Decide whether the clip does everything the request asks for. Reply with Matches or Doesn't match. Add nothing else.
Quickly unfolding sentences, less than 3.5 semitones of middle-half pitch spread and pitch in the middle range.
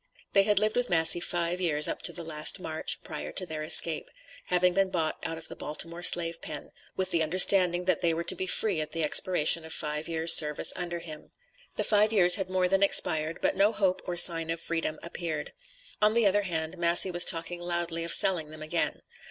Matches